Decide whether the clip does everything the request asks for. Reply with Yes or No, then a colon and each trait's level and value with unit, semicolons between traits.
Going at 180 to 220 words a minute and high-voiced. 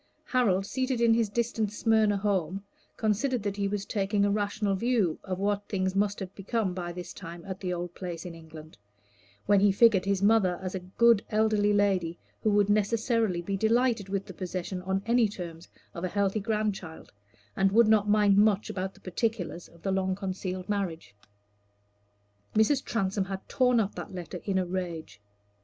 Yes: average, 185 wpm; high, 200 Hz